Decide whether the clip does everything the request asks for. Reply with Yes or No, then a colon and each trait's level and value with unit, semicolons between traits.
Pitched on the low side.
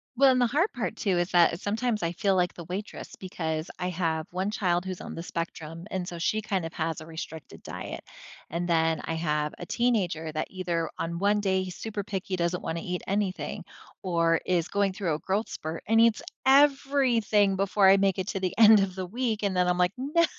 No: medium, 185 Hz